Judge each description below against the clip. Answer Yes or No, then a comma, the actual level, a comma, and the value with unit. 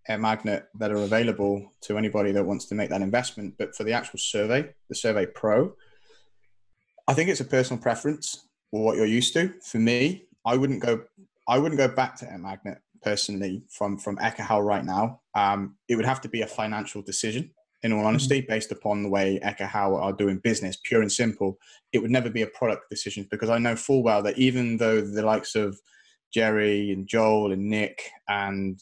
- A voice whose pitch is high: No, low, 110 Hz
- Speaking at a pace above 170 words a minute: Yes, fast, 205 wpm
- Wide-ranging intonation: No, average, 2.9 semitones